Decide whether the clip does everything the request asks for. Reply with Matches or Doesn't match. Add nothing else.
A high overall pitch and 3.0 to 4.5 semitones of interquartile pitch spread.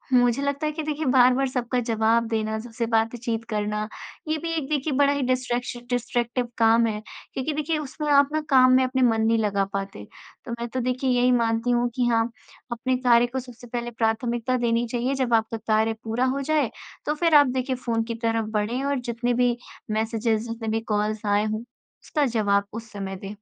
Doesn't match